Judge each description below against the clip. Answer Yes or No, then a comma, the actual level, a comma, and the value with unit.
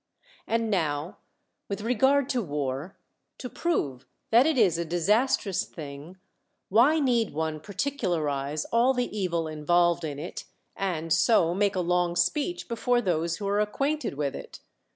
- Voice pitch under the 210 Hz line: Yes, medium, 185 Hz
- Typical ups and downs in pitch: No, wide, 6.6 semitones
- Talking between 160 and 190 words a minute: No, average, 150 wpm